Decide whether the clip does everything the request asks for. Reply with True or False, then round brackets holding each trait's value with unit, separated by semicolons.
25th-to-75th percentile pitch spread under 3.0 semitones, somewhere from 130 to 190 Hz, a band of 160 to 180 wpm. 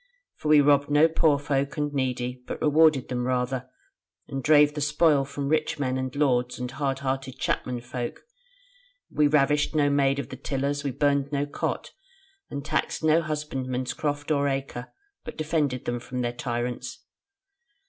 True (2.4 semitones; 140 Hz; 170 wpm)